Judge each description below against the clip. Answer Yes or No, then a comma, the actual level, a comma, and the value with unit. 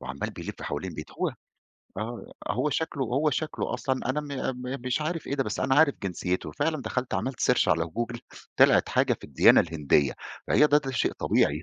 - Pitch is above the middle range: No, low, 130 Hz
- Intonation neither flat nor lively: No, wide, 8.2 semitones